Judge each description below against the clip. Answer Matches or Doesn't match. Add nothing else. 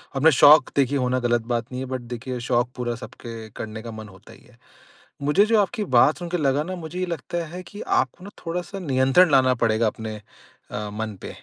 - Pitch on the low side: Matches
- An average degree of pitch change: Doesn't match